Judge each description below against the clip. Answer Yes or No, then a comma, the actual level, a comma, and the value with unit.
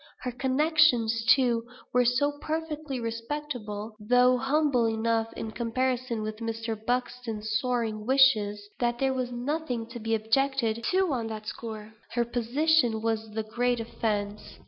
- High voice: Yes, high, 240 Hz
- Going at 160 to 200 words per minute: No, average, 140 wpm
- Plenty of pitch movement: No, average, 2.8 semitones